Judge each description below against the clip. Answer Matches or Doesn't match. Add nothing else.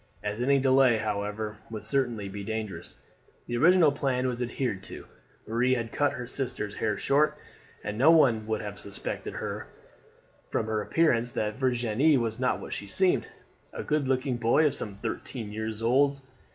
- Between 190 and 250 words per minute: Doesn't match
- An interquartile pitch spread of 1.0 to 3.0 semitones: Doesn't match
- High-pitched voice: Doesn't match